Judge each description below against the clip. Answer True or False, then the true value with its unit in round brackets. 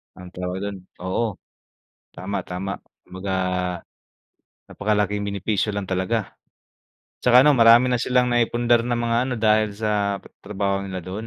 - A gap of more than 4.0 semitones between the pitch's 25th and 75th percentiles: False (3.1 semitones)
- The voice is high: False (105 Hz)